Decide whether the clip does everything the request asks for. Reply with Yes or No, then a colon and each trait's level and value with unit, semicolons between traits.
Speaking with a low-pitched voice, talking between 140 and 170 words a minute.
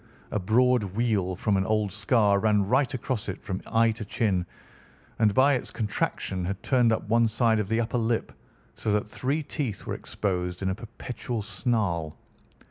No: low, 110 Hz; average, 180 wpm